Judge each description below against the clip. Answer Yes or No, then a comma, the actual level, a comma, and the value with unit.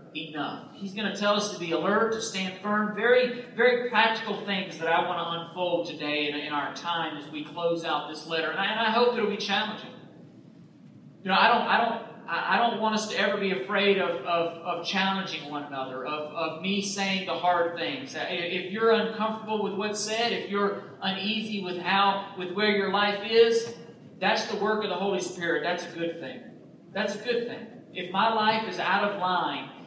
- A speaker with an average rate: No, fast, 210 wpm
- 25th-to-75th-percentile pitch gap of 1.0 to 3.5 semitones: No, average, 4.1 semitones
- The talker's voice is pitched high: Yes, high, 195 Hz